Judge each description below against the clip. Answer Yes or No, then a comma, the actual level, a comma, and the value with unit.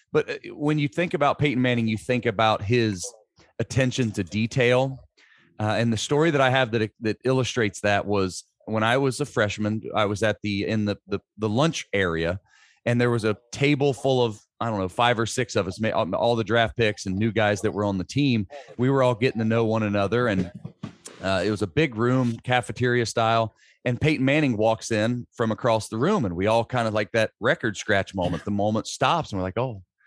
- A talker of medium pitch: No, low, 115 Hz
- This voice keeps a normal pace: No, fast, 220 wpm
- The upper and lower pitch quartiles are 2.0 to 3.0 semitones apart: No, average, 3.5 semitones